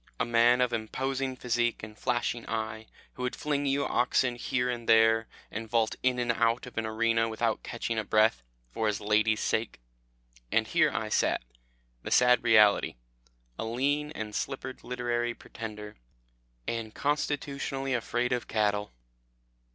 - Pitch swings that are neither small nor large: No, narrow, 2.3 semitones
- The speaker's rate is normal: Yes, average, 150 wpm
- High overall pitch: No, low, 120 Hz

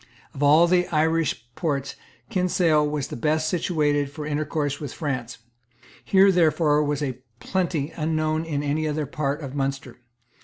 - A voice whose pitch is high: No, medium, 150 Hz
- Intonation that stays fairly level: Yes, narrow, 2.2 semitones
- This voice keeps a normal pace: Yes, average, 150 wpm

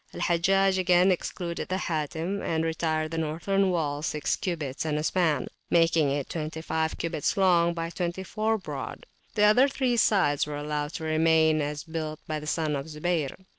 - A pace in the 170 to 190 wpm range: Yes, average, 175 wpm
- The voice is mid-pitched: Yes, medium, 165 Hz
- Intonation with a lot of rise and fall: No, average, 3.0 semitones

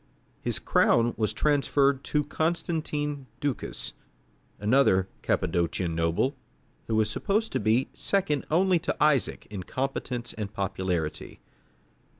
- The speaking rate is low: Yes, slow, 115 wpm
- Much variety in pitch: Yes, wide, 7.0 semitones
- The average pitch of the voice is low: Yes, low, 130 Hz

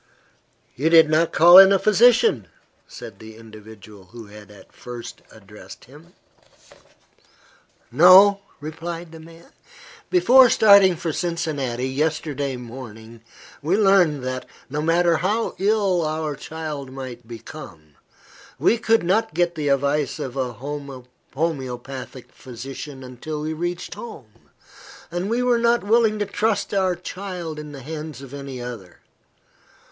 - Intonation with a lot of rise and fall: Yes, wide, 5.9 semitones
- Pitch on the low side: No, medium, 155 Hz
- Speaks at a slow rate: Yes, slow, 130 wpm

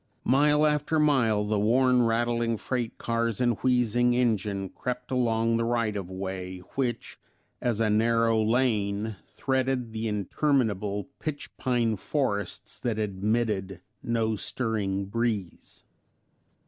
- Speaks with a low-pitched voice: Yes, low, 115 Hz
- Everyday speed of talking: No, slow, 120 wpm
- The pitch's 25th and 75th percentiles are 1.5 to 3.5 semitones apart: Yes, average, 3.0 semitones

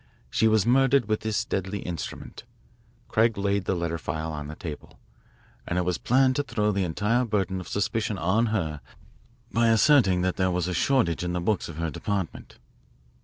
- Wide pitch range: No, average, 4.2 semitones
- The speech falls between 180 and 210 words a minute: Yes, average, 185 wpm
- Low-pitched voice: Yes, low, 100 Hz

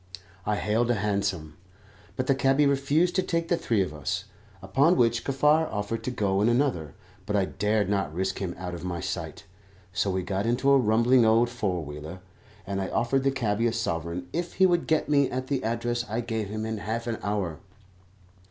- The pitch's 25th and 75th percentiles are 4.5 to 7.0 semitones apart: Yes, average, 5.2 semitones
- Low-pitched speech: Yes, low, 110 Hz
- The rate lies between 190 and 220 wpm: Yes, fast, 205 wpm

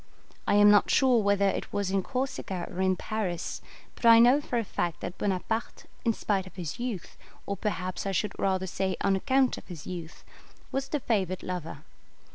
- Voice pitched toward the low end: No, high, 195 Hz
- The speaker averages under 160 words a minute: No, average, 195 wpm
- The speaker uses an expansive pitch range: No, average, 3.8 semitones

